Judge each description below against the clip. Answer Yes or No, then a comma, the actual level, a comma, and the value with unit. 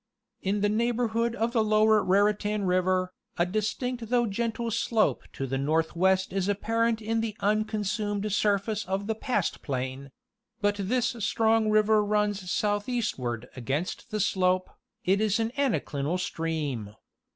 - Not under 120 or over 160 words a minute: Yes, slow, 135 wpm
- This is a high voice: Yes, high, 205 Hz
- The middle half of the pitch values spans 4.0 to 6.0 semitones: No, average, 3.3 semitones